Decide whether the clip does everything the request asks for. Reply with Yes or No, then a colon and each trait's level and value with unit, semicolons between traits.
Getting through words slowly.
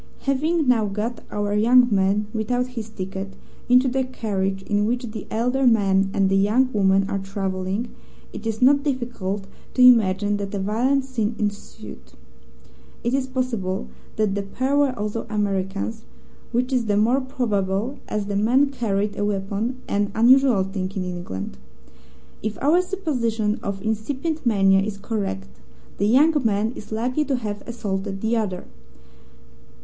No: average, 155 wpm